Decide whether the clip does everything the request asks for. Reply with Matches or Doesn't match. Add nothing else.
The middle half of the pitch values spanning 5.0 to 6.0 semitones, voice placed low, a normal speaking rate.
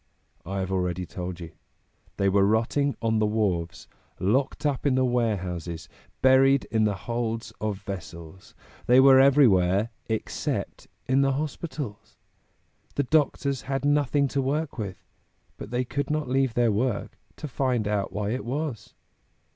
Matches